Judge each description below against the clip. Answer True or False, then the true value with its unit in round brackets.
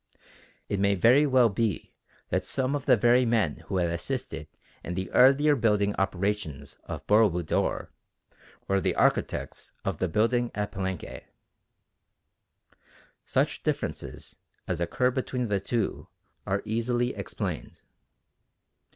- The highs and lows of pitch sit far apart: False (4.5 semitones)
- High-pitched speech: False (105 Hz)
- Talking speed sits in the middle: False (125 wpm)